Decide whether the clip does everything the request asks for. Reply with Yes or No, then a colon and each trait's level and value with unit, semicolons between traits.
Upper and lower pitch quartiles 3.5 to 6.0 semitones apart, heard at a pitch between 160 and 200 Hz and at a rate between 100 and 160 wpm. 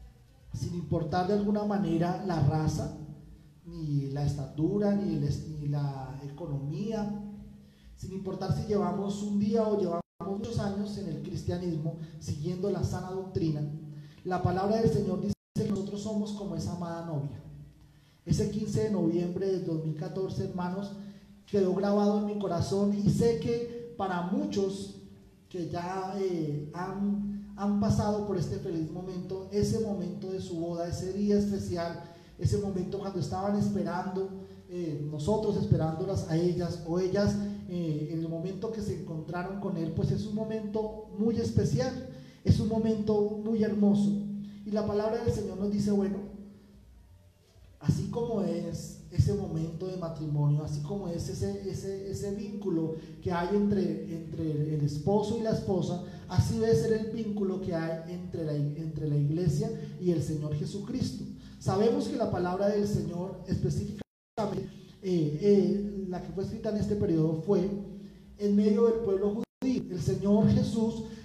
Yes: average, 3.8 semitones; medium, 185 Hz; average, 155 wpm